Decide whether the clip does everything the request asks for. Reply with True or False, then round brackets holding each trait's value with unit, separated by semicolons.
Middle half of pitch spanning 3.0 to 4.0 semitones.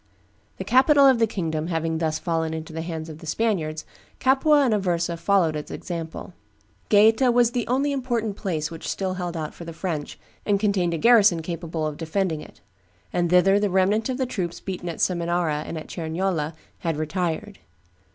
False (4.5 semitones)